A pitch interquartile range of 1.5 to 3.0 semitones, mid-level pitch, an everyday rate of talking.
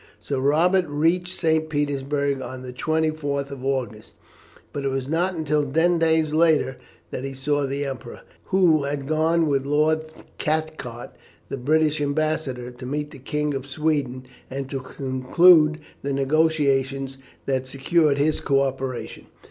Yes: average, 2.7 semitones; medium, 145 Hz; average, 150 wpm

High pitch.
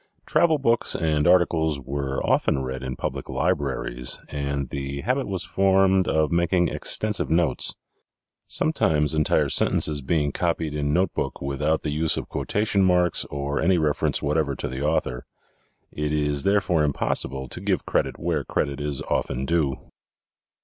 No: very low, 75 Hz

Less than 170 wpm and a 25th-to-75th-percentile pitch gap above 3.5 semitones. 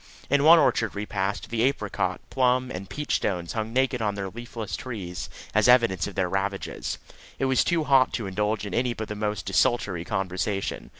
No: average, 190 wpm; average, 4.4 semitones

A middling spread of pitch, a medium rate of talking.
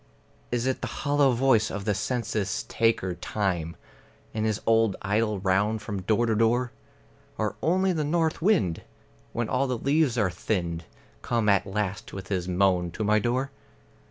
Yes: average, 4.3 semitones; average, 165 wpm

